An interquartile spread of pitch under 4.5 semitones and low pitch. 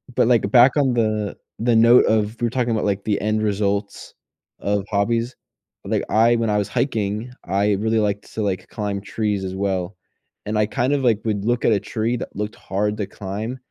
Yes: narrow, 2.4 semitones; low, 105 Hz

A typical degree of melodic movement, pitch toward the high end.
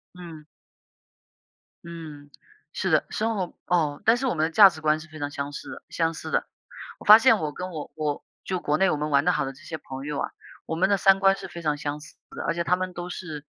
No: average, 3.7 semitones; medium, 160 Hz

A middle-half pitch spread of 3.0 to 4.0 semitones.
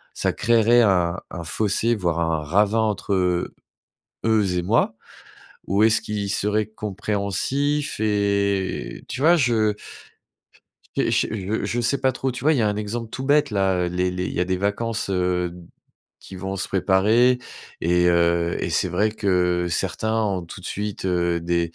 Yes: average, 3.7 semitones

